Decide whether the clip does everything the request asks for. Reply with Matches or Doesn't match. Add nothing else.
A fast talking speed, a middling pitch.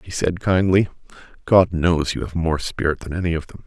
Doesn't match